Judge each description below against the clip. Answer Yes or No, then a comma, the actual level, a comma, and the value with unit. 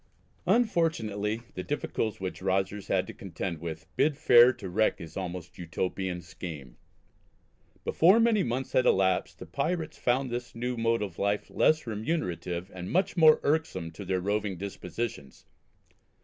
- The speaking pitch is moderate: No, low, 105 Hz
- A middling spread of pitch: No, wide, 5.9 semitones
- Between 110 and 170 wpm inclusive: Yes, average, 150 wpm